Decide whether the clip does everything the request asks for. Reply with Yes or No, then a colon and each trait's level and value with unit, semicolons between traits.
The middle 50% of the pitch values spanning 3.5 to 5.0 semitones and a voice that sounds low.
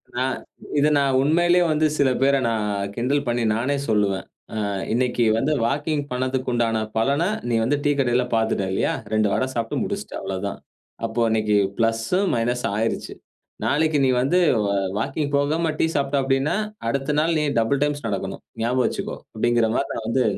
Yes: average, 4.0 semitones; low, 130 Hz